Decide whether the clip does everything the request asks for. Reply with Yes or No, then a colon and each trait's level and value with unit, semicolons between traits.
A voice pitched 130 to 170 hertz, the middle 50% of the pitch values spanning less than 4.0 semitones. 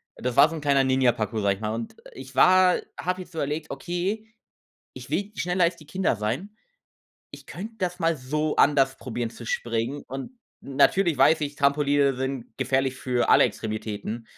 No: medium, 140 Hz; wide, 5.4 semitones